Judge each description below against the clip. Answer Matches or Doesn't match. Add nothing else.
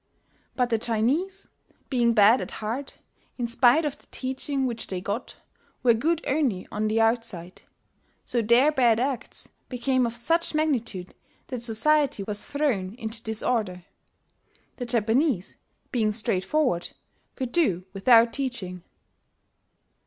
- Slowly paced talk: Matches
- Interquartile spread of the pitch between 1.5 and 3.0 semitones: Doesn't match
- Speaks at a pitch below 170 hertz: Doesn't match